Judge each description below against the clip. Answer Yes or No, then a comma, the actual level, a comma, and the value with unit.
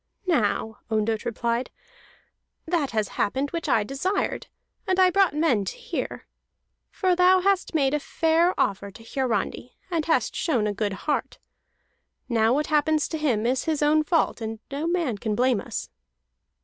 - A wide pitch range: Yes, wide, 6.7 semitones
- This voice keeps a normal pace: Yes, average, 160 wpm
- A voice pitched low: No, very high, 280 Hz